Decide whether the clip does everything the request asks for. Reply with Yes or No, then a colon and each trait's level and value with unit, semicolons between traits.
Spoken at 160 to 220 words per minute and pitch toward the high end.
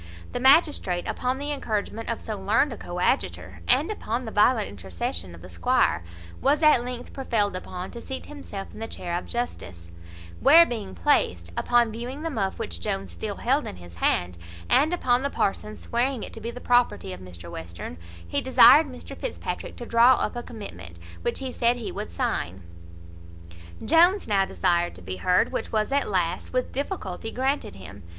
Yes: average, 185 wpm; high, 220 Hz